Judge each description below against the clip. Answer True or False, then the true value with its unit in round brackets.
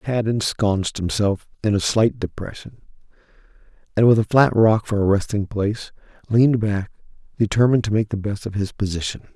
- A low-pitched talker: True (105 Hz)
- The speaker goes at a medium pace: True (165 wpm)